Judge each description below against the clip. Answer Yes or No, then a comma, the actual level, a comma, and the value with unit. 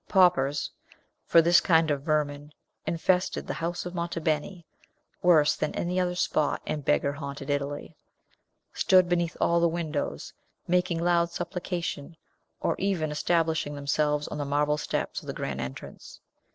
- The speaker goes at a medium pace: Yes, average, 150 wpm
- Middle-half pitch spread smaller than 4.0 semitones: Yes, average, 3.0 semitones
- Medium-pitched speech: Yes, medium, 165 Hz